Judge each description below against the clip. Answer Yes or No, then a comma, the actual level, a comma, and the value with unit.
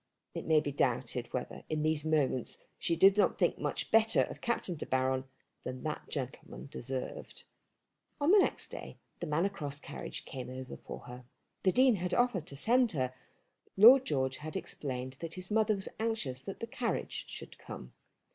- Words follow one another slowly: No, average, 185 wpm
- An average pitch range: No, wide, 8.1 semitones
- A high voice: No, medium, 155 Hz